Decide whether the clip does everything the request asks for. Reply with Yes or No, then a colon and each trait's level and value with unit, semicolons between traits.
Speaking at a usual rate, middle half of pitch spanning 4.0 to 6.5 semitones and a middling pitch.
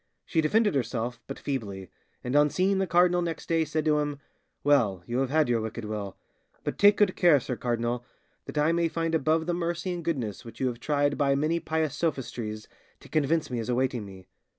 No: fast, 210 wpm; wide, 5.6 semitones; medium, 145 Hz